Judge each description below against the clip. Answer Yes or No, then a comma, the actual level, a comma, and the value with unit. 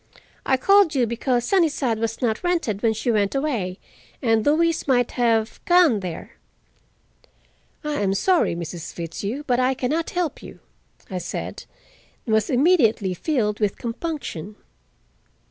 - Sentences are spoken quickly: No, average, 145 wpm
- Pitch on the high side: Yes, high, 245 Hz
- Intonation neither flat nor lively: No, wide, 6.1 semitones